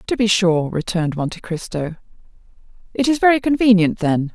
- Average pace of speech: Yes, average, 150 wpm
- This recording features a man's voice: No, female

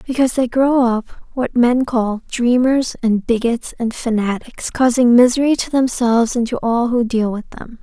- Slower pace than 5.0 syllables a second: Yes, 4.6 syllables/s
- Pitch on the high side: Yes, high, 240 Hz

